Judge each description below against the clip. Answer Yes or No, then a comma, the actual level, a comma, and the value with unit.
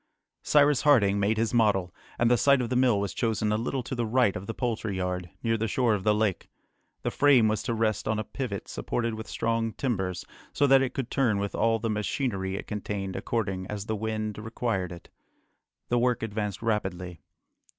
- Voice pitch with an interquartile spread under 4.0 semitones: Yes, average, 3.0 semitones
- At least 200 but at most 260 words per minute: Yes, fast, 205 wpm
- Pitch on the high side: No, low, 110 Hz